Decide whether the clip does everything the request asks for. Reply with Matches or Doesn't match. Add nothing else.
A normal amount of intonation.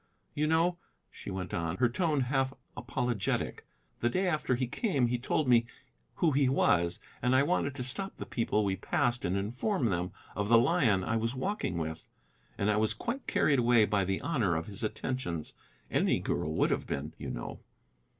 Doesn't match